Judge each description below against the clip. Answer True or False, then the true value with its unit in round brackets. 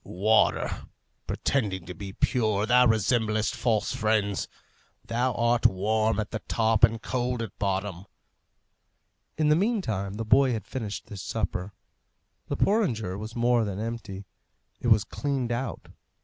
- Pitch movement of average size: True (3.0 semitones)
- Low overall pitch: True (110 Hz)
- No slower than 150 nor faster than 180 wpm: False (140 wpm)